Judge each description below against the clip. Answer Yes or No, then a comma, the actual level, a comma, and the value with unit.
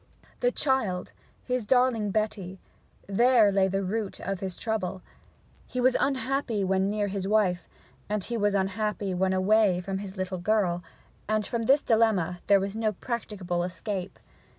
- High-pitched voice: Yes, high, 200 Hz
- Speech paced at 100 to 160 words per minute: Yes, average, 150 wpm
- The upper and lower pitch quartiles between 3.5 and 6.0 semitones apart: No, average, 2.9 semitones